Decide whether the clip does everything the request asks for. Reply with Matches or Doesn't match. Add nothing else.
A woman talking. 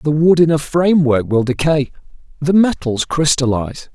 Doesn't match